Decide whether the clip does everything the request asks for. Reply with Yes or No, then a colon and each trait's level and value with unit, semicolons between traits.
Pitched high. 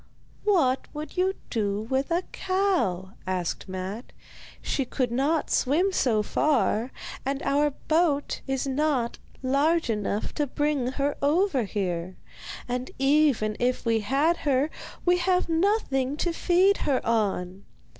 Yes: very high, 275 Hz